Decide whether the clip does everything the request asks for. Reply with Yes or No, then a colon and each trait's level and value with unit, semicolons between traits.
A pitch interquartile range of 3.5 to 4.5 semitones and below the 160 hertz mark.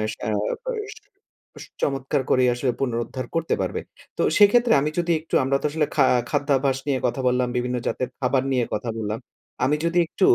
Yes: average, 3.8 semitones; low, 135 Hz